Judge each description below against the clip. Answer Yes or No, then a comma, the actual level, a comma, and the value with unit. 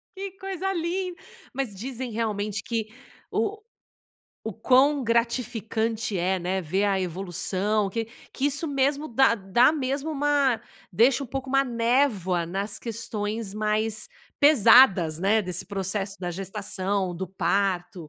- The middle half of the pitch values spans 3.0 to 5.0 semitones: No, wide, 5.5 semitones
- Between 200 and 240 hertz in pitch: Yes, high, 220 Hz